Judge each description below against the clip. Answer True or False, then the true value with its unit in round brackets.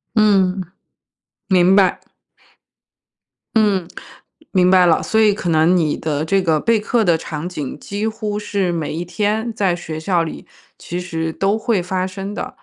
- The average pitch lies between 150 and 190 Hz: True (185 Hz)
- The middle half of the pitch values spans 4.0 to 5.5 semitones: False (3.6 semitones)